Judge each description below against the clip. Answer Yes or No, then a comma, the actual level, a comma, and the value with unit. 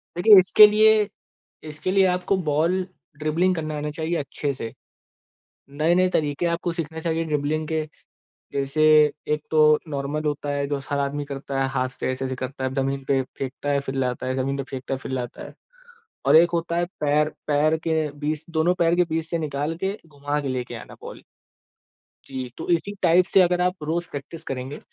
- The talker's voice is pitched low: No, medium, 150 Hz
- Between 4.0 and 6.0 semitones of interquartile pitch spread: No, average, 3.4 semitones